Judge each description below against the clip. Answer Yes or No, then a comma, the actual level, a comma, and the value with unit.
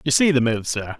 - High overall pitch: No, low, 130 Hz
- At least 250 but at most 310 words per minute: Yes, fast, 305 wpm